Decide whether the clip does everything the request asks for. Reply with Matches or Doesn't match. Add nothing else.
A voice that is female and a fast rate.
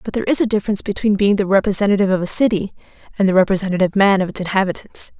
Matches